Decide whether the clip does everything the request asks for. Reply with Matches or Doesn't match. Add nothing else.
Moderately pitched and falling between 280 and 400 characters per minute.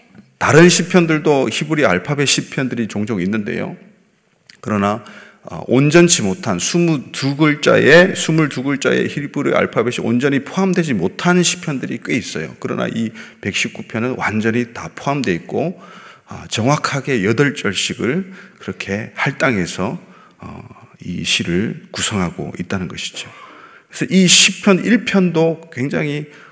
Doesn't match